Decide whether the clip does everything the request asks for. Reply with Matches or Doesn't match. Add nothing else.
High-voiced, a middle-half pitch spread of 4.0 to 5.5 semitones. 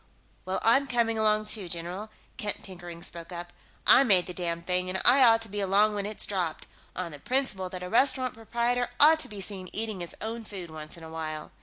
Matches